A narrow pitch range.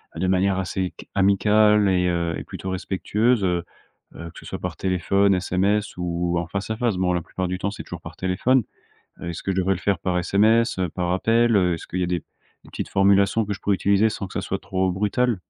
Yes: narrow, 2.3 semitones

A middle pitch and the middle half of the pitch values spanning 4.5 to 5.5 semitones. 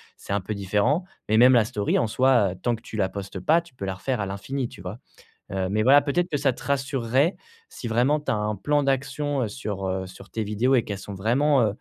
No: low, 115 Hz; average, 5.2 semitones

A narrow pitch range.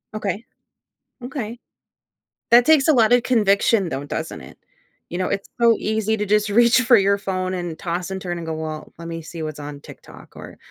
No: average, 5.2 semitones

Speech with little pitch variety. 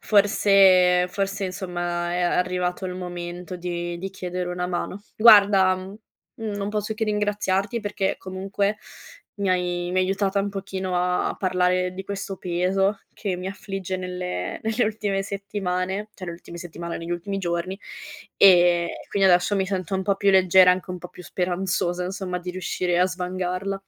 Yes: narrow, 1.7 semitones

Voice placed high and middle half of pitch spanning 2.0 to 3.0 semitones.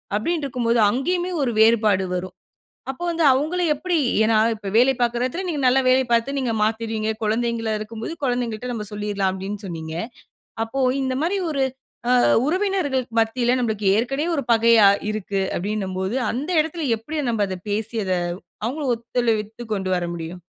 No: high, 230 Hz; average, 4.2 semitones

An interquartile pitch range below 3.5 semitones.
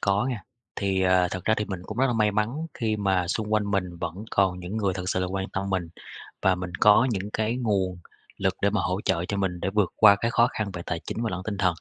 Yes: average, 2.7 semitones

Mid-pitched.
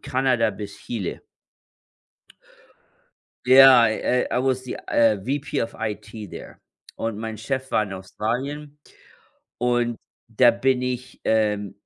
No: low, 120 Hz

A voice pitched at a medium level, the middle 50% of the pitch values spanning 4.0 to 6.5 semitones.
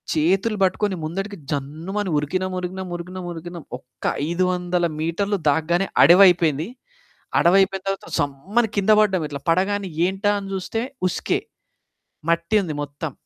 No: medium, 180 Hz; average, 3.0 semitones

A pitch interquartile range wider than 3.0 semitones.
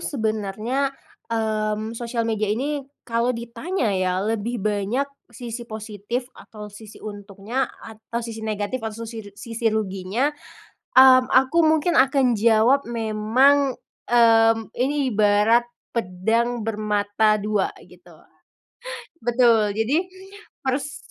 No: average, 2.7 semitones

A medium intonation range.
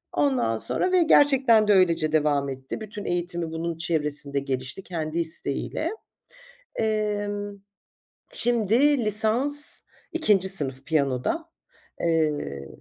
No: wide, 6.4 semitones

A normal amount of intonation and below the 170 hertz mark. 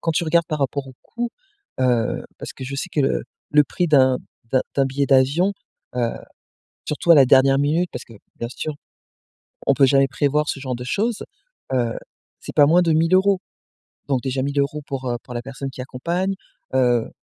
Yes: average, 3.3 semitones; medium, 140 Hz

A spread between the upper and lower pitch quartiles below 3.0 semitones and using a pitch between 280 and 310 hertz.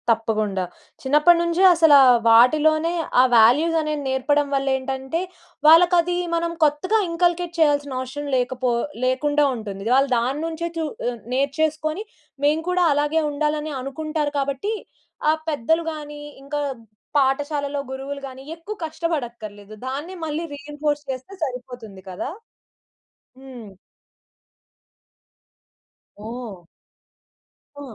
No: average, 3.4 semitones; very high, 290 Hz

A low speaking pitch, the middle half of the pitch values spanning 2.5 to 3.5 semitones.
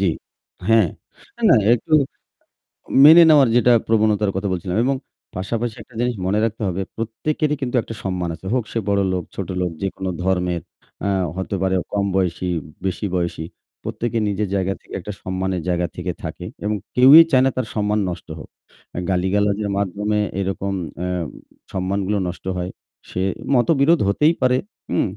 No: low, 100 Hz; average, 3.9 semitones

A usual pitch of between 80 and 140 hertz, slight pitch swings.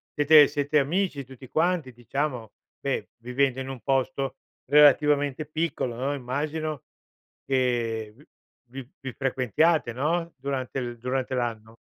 No: low, 135 Hz; average, 3.0 semitones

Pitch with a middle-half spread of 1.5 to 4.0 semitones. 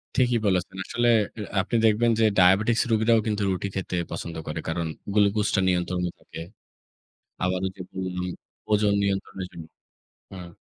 Yes: average, 2.9 semitones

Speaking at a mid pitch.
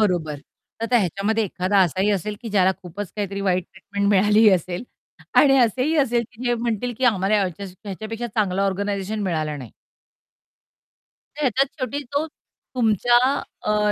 No: high, 205 Hz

